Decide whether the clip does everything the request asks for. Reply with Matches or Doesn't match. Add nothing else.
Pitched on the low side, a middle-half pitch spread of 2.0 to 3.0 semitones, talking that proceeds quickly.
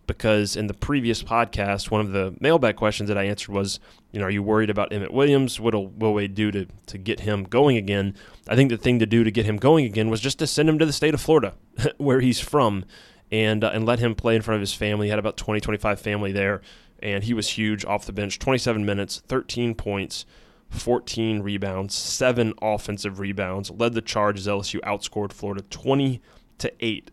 Matches